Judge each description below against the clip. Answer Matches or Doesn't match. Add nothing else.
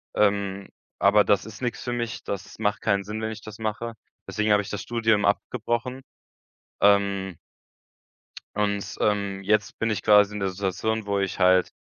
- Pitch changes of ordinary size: Doesn't match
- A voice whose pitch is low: Matches